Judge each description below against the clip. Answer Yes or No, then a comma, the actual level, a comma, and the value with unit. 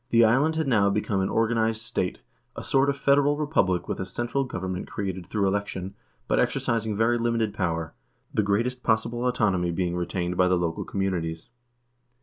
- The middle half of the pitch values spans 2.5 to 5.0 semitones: Yes, average, 4.3 semitones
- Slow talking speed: No, average, 175 wpm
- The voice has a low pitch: Yes, low, 105 Hz